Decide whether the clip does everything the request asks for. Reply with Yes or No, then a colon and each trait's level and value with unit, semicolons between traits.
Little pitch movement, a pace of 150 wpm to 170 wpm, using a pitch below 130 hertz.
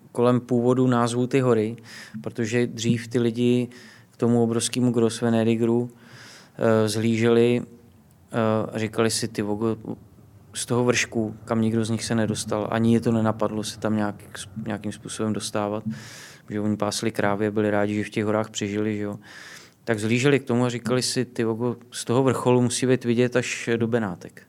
Yes: narrow, 2.0 semitones; average, 165 wpm; low, 115 Hz